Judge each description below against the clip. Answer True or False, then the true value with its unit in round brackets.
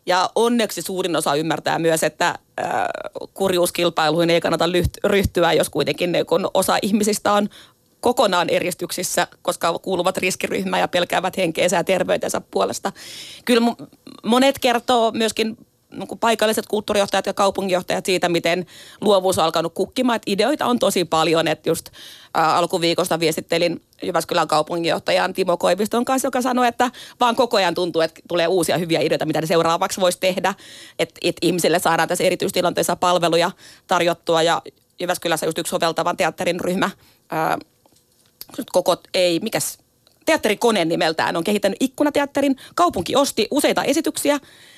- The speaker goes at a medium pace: True (135 wpm)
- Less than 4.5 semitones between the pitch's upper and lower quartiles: False (4.8 semitones)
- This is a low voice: False (185 Hz)